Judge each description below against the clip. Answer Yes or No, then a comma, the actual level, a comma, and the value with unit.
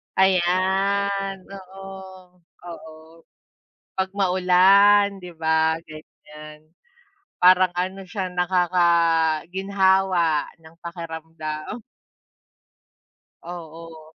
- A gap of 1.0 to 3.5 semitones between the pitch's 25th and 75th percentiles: Yes, average, 2.8 semitones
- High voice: No, medium, 180 Hz